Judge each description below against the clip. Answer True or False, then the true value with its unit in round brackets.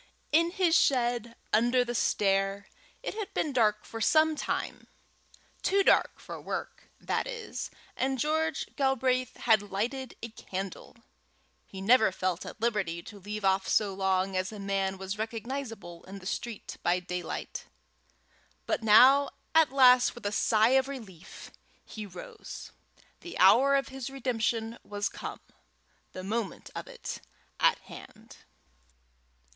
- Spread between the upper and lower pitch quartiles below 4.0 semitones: False (5.1 semitones)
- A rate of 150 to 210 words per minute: False (140 wpm)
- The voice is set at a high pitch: True (225 Hz)